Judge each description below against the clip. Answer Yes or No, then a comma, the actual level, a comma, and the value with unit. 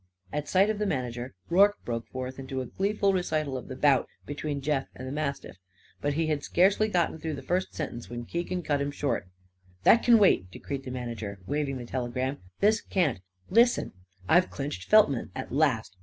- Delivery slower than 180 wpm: No, average, 190 wpm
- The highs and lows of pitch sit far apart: Yes, wide, 5.8 semitones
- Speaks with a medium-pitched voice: Yes, medium, 145 Hz